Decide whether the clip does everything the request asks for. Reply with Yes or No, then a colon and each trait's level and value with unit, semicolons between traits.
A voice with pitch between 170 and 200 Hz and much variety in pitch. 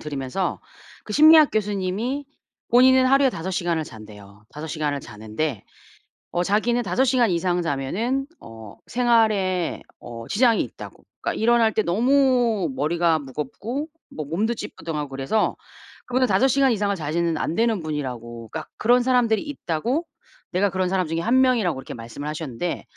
Yes: medium, 185 Hz; wide, 8.0 semitones